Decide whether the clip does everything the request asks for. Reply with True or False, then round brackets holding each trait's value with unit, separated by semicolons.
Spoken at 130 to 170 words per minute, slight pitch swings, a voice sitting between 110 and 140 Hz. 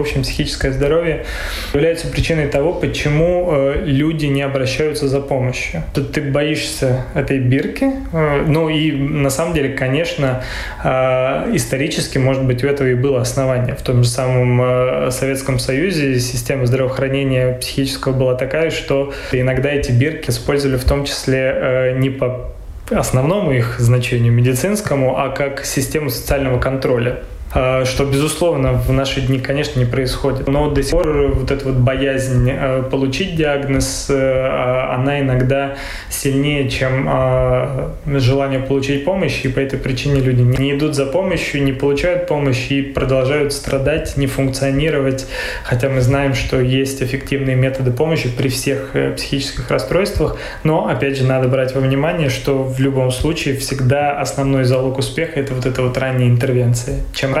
True (145 wpm; 1.4 semitones; 135 Hz)